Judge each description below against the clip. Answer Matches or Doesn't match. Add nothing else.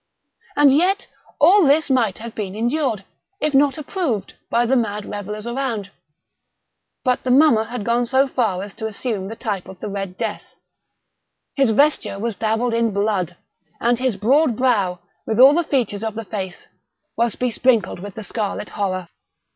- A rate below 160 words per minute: Doesn't match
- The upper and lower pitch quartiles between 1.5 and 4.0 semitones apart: Doesn't match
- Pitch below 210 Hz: Doesn't match